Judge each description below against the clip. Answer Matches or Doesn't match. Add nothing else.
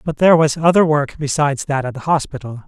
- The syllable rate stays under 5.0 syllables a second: Doesn't match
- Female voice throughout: Doesn't match